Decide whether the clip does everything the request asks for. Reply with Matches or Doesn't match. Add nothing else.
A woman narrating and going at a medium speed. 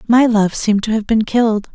Doesn't match